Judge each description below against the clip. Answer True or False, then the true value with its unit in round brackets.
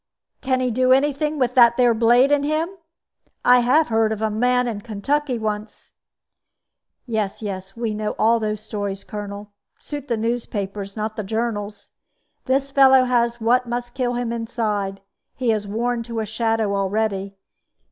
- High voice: True (230 Hz)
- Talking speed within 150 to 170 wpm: True (165 wpm)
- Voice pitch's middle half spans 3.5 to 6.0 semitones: False (2.9 semitones)